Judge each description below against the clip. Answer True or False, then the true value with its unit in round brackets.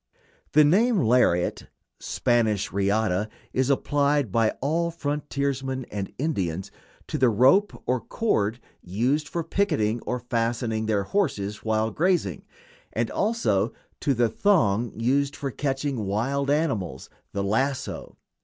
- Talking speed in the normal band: False (125 wpm)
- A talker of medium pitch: False (125 Hz)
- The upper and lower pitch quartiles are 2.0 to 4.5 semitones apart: False (5.2 semitones)